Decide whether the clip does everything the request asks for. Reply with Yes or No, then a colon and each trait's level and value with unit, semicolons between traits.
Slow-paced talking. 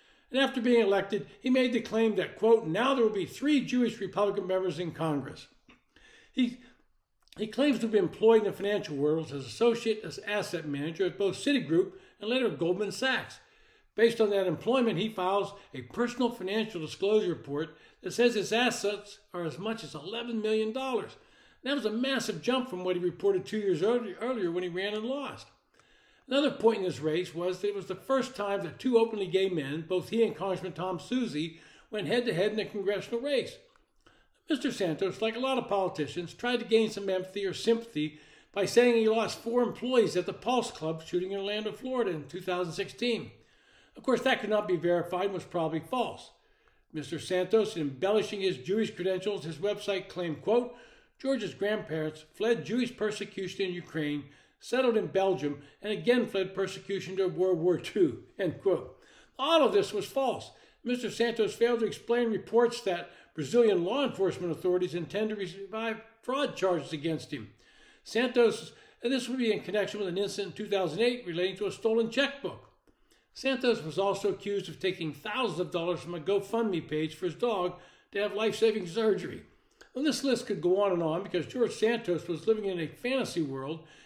No: average, 185 wpm